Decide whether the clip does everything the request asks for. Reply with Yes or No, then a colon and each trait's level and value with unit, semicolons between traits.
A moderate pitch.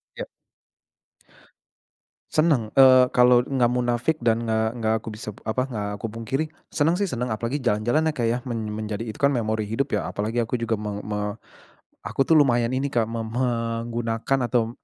No: low, 120 Hz